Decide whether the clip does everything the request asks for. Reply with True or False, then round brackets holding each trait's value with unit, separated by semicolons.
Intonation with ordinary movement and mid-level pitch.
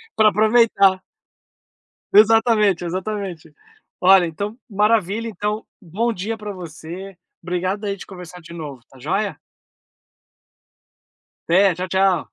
False (3.1 semitones; 195 Hz)